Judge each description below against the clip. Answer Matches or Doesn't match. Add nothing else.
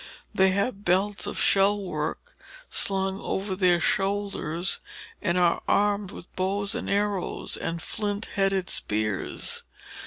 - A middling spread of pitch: Doesn't match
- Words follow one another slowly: Matches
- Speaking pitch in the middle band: Doesn't match